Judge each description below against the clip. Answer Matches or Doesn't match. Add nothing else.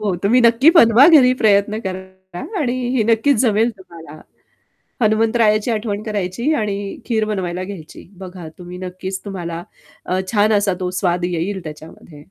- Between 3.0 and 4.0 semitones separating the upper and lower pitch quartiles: Matches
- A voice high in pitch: Matches